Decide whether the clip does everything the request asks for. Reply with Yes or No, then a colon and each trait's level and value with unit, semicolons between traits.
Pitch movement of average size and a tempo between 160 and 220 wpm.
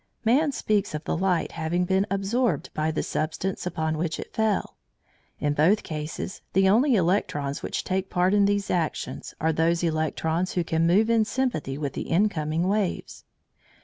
Yes: average, 4.2 semitones; average, 170 wpm